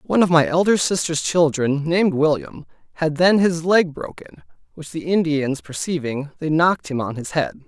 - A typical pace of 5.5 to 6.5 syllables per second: No, 5.3 syllables/s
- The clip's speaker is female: No, male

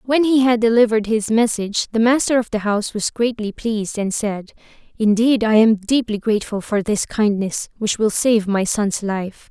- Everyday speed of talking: Yes, average, 190 wpm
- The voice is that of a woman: Yes, female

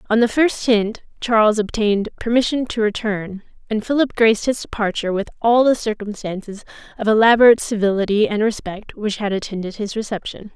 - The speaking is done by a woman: Yes, female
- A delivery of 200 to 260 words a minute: No, average, 160 wpm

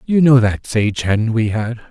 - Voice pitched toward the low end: Yes, low, 115 Hz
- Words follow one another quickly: Yes, fast, 220 wpm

